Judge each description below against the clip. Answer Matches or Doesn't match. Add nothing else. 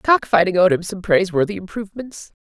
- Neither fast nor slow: Matches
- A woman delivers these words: Matches